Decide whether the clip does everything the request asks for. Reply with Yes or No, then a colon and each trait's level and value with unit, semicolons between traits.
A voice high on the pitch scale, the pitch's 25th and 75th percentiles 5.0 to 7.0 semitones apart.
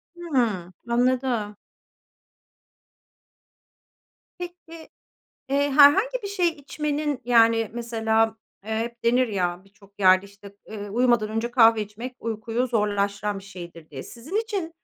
Yes: high, 230 Hz; wide, 5.4 semitones